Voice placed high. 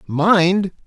No: medium, 180 Hz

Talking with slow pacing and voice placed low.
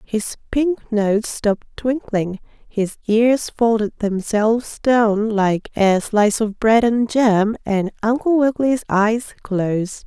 No: slow, 130 wpm; high, 220 Hz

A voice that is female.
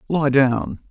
No: male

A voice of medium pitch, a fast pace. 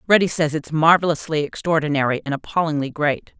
No: medium, 155 Hz; average, 140 wpm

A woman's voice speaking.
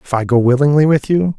No: male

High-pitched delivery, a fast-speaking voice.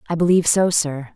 No: medium, 165 Hz; fast, 210 wpm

